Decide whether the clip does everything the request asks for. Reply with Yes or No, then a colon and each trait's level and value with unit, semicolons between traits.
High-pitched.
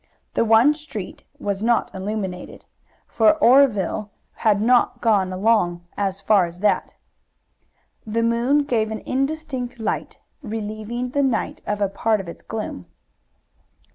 Yes: high, 220 Hz